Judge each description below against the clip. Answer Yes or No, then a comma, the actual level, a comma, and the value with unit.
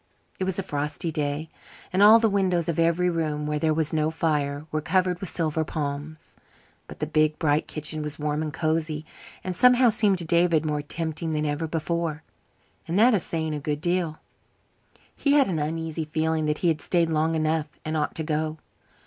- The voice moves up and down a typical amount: No, narrow, 2.0 semitones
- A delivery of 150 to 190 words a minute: No, average, 200 wpm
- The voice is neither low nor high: Yes, medium, 160 Hz